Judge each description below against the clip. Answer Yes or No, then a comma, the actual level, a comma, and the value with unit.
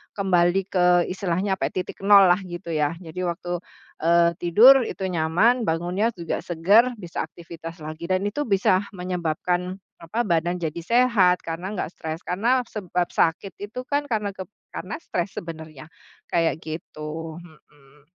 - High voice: No, medium, 175 Hz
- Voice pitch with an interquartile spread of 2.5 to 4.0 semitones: Yes, average, 3.0 semitones